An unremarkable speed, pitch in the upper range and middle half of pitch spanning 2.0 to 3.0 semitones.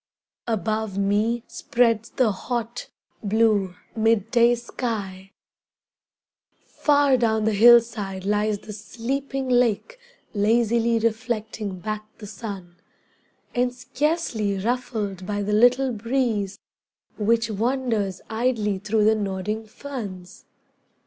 No: slow, 105 wpm; high, 220 Hz; average, 2.7 semitones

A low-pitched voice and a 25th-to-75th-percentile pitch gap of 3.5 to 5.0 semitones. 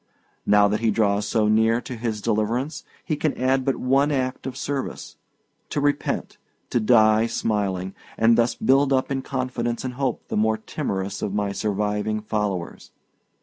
Yes: low, 115 Hz; average, 3.8 semitones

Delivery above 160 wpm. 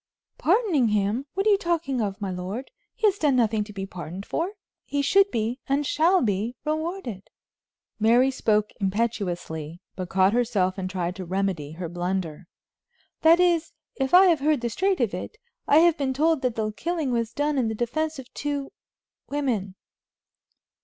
Yes: average, 175 wpm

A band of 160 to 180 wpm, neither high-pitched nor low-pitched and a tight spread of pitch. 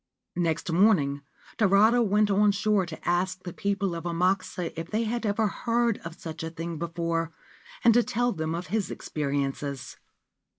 No: average, 165 wpm; medium, 180 Hz; average, 4.2 semitones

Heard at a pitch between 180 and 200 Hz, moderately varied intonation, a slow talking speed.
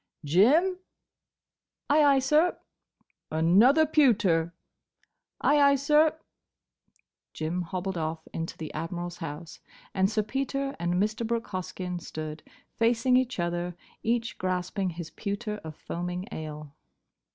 No: high, 190 Hz; wide, 7.0 semitones; slow, 120 wpm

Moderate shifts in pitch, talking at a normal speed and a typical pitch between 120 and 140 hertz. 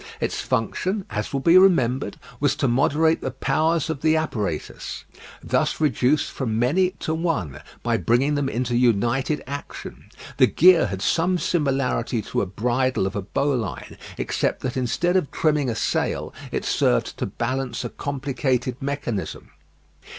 Yes: average, 4.6 semitones; average, 150 wpm; low, 135 Hz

